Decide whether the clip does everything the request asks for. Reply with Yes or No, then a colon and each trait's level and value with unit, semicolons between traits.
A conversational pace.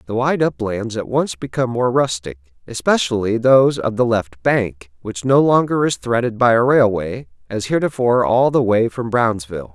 Yes: average, 180 wpm